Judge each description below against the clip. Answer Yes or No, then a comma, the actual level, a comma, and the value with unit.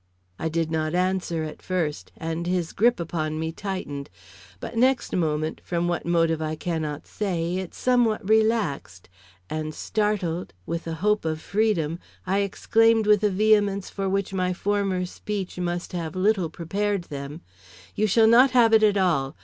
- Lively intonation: No, average, 4.3 semitones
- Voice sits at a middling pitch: Yes, medium, 180 Hz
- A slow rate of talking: No, average, 165 wpm